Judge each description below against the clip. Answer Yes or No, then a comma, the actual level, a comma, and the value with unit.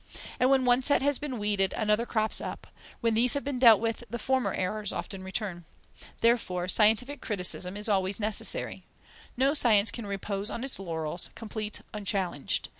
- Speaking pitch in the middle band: No, high, 215 Hz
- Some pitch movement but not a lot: Yes, average, 3.8 semitones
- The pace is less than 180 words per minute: Yes, average, 170 wpm